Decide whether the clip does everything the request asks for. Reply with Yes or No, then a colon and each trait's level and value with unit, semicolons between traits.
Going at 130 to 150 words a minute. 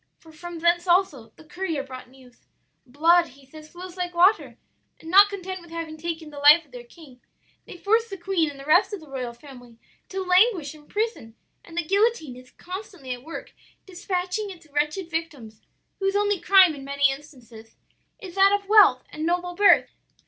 No: average, 190 wpm